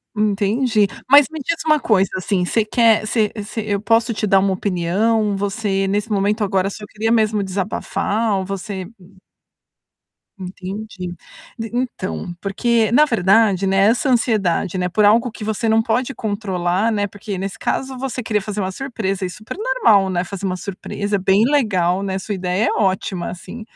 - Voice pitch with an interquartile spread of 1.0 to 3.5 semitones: Yes, average, 2.8 semitones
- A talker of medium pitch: No, high, 205 Hz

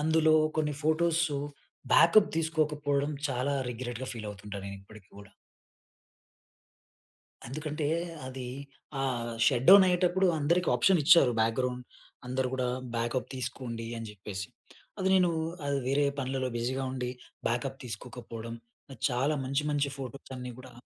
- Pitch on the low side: Yes, low, 130 Hz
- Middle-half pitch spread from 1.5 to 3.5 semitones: No, average, 4.2 semitones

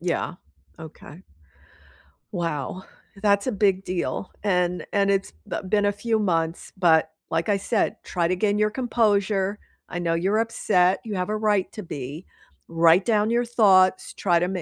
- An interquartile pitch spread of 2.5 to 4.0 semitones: Yes, average, 3.2 semitones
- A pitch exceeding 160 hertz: Yes, high, 190 Hz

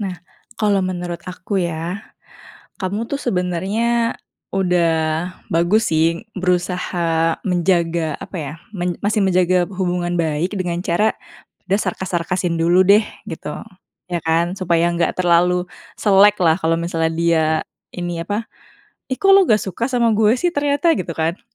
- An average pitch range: Yes, average, 3.0 semitones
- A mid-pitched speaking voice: Yes, medium, 180 Hz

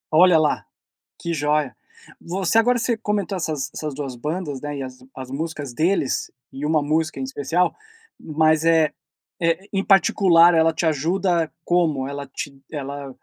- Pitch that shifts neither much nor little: Yes, average, 3.6 semitones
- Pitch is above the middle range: No, medium, 160 Hz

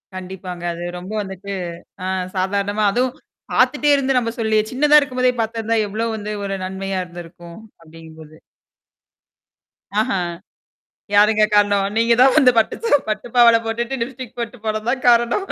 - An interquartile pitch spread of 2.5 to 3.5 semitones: No, average, 4.1 semitones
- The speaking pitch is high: Yes, high, 215 Hz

